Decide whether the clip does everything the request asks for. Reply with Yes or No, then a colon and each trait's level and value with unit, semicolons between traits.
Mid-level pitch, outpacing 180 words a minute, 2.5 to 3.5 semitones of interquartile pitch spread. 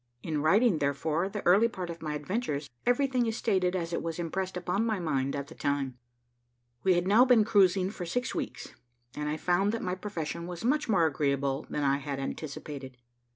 No: medium, 175 Hz; average, 200 wpm; wide, 5.5 semitones